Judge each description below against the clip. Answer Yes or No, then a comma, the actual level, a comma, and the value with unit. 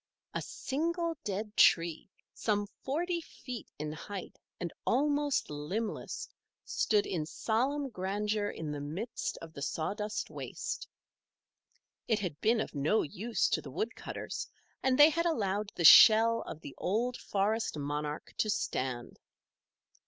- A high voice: Yes, high, 210 Hz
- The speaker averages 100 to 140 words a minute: Yes, slow, 135 wpm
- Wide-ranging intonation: Yes, wide, 7.0 semitones